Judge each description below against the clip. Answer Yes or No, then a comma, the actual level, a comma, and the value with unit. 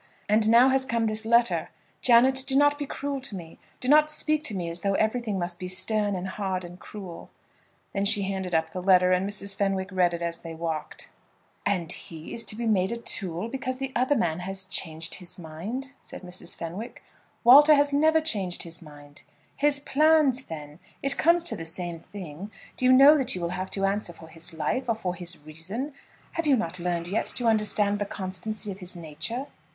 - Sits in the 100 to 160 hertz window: No, high, 200 Hz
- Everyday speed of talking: No, fast, 210 wpm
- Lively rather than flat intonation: Yes, wide, 6.3 semitones